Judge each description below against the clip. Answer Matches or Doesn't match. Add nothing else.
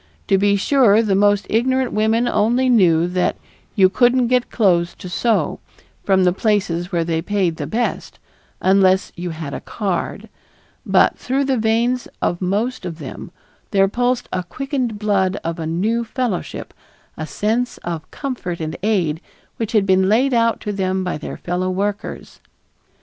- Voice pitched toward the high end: Matches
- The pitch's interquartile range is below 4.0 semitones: Doesn't match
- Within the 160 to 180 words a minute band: Matches